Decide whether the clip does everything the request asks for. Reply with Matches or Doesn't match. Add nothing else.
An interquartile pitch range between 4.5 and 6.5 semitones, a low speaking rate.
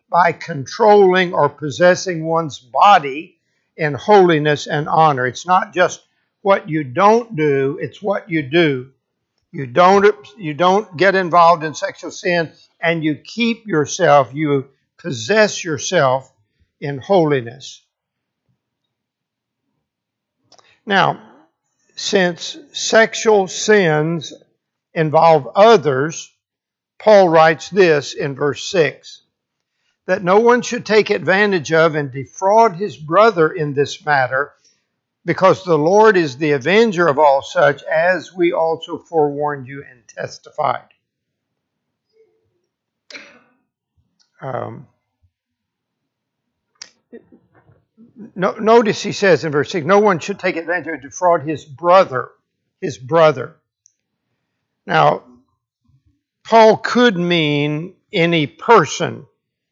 Matches